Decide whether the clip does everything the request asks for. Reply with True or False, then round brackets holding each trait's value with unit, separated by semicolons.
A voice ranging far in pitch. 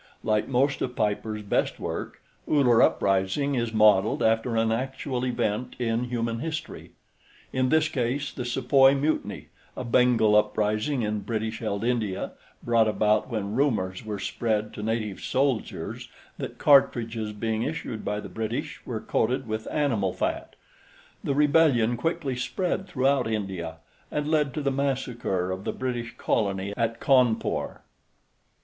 False (3.8 semitones)